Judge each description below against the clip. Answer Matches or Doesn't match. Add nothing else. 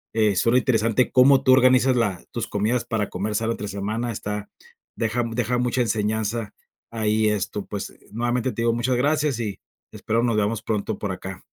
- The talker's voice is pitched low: Matches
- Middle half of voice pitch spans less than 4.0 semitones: Matches